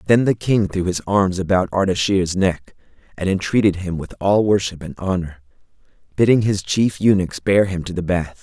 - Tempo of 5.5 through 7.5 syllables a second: No, 5.0 syllables/s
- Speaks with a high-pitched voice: No, very low, 95 Hz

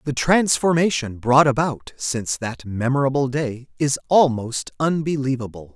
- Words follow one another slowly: Yes, slow, 115 wpm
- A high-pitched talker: No, low, 135 Hz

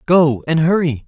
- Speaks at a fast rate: No, average, 165 wpm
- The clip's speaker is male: Yes, male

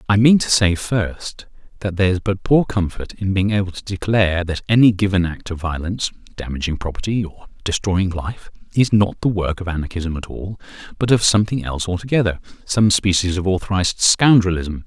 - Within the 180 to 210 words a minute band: No, average, 165 wpm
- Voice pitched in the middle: No, very low, 95 Hz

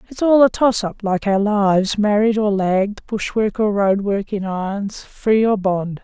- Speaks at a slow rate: No, average, 180 wpm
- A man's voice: No, female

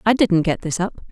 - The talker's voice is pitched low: No, high, 190 Hz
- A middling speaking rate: No, fast, 270 wpm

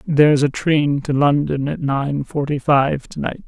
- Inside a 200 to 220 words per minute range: Yes, fast, 205 wpm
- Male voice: No, female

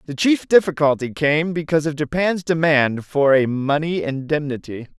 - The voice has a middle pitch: Yes, medium, 150 Hz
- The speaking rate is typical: Yes, average, 145 wpm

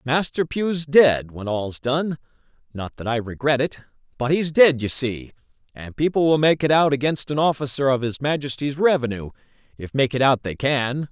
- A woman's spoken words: No, male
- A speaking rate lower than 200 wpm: Yes, average, 190 wpm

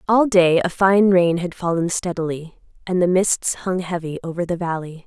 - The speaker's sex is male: No, female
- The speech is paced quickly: No, average, 190 wpm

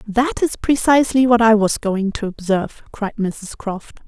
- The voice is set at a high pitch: Yes, high, 220 Hz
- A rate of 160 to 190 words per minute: Yes, average, 175 wpm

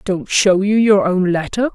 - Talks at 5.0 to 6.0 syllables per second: No, 4.3 syllables/s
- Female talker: Yes, female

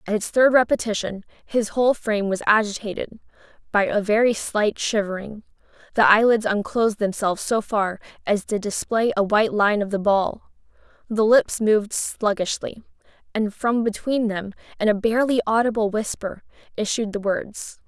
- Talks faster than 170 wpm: No, average, 150 wpm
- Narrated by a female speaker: Yes, female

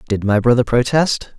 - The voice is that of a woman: No, male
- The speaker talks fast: No, average, 175 wpm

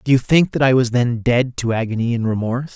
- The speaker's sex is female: No, male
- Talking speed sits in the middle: No, fast, 260 wpm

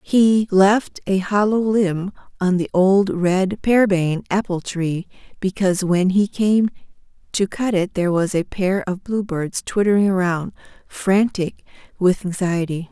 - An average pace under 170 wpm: Yes, average, 140 wpm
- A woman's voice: Yes, female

